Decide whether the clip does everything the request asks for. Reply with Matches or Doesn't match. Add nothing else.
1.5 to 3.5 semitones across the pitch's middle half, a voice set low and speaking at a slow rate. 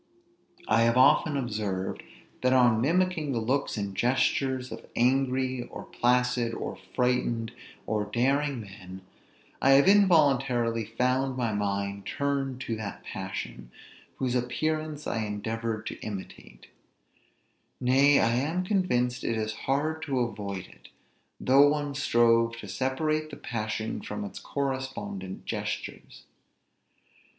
Doesn't match